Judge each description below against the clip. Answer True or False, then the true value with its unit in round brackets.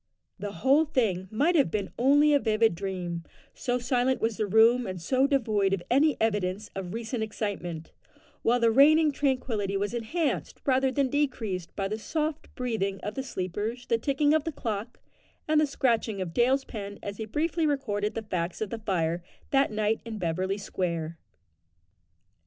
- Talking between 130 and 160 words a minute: False (175 wpm)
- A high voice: True (225 Hz)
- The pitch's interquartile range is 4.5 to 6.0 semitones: True (5.3 semitones)